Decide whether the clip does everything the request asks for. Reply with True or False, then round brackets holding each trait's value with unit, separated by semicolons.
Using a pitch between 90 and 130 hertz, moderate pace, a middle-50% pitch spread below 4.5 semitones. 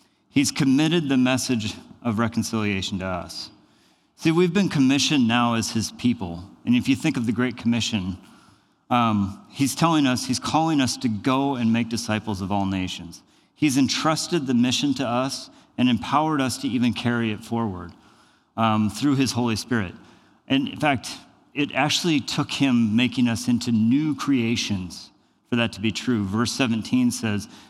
True (120 Hz; 170 wpm; 3.6 semitones)